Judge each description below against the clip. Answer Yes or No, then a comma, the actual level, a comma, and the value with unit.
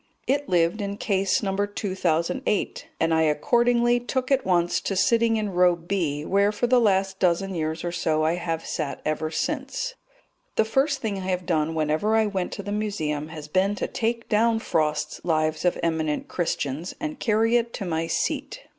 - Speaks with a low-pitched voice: No, high, 190 Hz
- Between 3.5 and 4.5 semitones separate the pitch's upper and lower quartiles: No, average, 5.3 semitones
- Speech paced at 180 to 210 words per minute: Yes, average, 185 wpm